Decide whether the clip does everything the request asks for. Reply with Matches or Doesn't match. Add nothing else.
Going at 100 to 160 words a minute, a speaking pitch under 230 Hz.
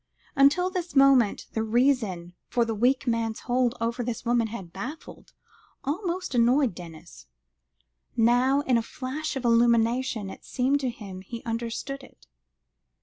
Doesn't match